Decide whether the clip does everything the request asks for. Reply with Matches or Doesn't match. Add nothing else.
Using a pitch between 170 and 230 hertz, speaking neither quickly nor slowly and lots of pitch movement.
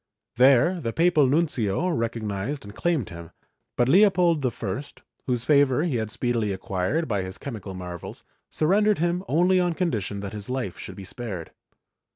Doesn't match